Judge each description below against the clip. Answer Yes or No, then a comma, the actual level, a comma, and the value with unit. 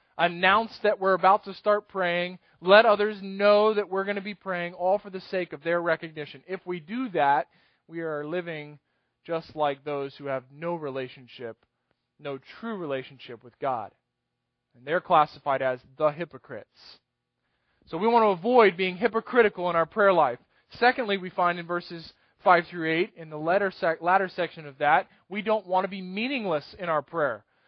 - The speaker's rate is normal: Yes, average, 180 wpm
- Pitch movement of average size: Yes, average, 4.7 semitones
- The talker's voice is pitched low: No, medium, 175 Hz